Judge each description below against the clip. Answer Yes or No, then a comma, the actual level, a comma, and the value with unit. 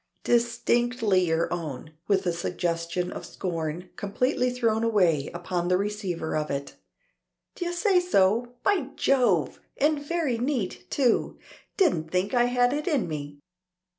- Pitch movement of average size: No, wide, 6.6 semitones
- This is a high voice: Yes, high, 205 Hz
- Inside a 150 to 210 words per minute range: No, slow, 135 wpm